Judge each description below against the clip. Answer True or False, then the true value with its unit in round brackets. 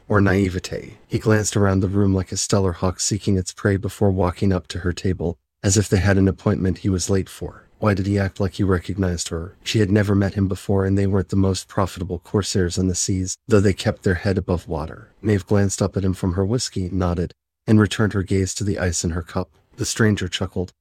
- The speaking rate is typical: False (240 wpm)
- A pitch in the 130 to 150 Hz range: False (95 Hz)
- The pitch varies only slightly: True (1.7 semitones)